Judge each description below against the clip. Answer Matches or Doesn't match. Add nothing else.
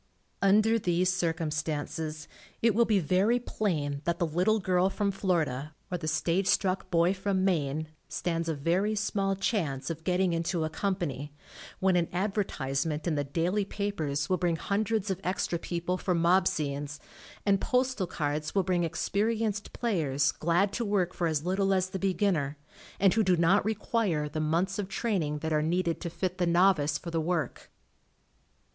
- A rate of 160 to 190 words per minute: Matches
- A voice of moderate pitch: Matches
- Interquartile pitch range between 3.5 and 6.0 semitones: Matches